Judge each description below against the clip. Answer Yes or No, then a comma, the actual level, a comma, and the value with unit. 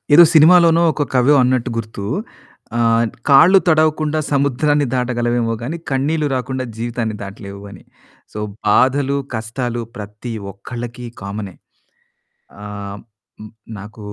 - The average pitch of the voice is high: No, low, 125 Hz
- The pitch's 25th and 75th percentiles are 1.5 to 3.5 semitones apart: No, average, 4.5 semitones